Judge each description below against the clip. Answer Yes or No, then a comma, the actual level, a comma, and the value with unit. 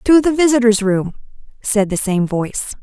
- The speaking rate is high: No, average, 170 wpm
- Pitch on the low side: No, high, 225 Hz